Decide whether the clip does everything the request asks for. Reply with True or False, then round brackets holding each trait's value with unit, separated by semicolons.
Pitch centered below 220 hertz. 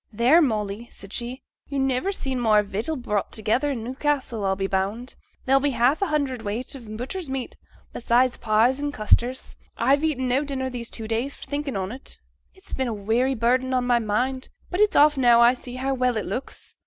False (250 Hz)